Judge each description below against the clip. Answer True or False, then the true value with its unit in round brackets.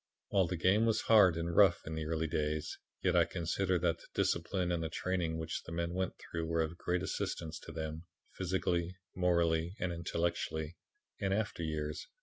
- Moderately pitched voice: False (85 Hz)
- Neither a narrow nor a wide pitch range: False (2.1 semitones)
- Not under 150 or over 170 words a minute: False (185 wpm)